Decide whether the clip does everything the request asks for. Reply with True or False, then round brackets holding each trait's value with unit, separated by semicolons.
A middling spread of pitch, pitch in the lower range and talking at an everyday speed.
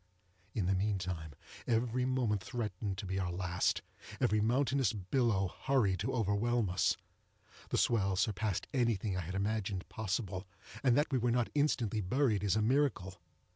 True (4.2 semitones; 105 Hz; 150 wpm)